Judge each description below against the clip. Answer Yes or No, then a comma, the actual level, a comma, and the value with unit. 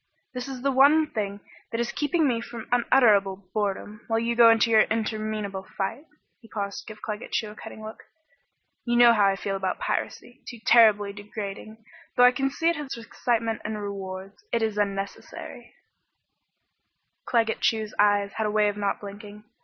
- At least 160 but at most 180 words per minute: No, average, 190 wpm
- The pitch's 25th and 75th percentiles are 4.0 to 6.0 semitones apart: No, narrow, 2.6 semitones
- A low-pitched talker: No, high, 215 Hz